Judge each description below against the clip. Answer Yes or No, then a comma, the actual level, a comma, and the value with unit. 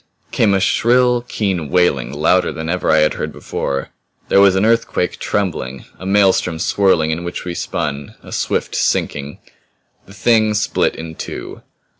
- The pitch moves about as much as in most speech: Yes, average, 4.4 semitones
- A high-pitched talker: No, very low, 90 Hz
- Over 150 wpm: Yes, average, 160 wpm